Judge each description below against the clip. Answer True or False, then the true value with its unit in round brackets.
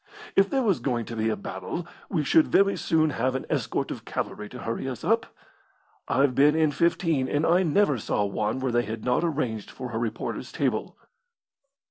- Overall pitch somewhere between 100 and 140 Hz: True (135 Hz)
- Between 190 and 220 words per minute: True (195 wpm)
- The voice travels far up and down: True (6.2 semitones)